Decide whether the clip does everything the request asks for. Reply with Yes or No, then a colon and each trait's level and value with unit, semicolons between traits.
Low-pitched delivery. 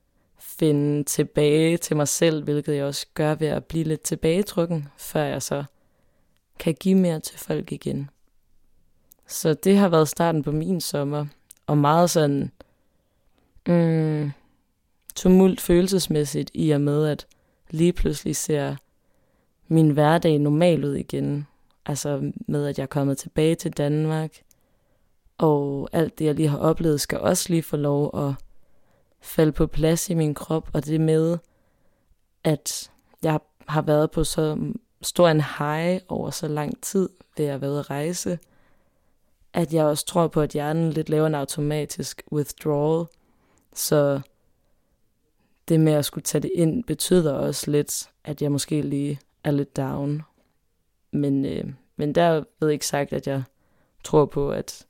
No: medium, 155 Hz